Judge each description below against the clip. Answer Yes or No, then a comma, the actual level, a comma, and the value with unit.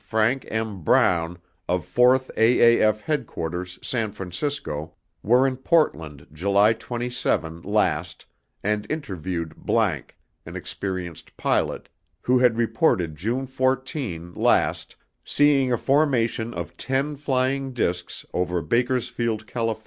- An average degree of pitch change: No, wide, 6.4 semitones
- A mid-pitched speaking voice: No, low, 115 Hz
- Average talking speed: No, slow, 115 wpm